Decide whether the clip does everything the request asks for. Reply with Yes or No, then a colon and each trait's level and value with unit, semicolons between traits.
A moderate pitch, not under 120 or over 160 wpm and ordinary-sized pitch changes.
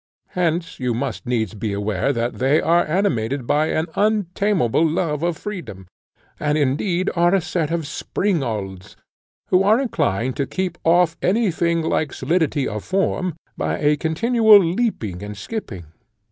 No: medium, 160 Hz; average, 150 wpm; wide, 6.6 semitones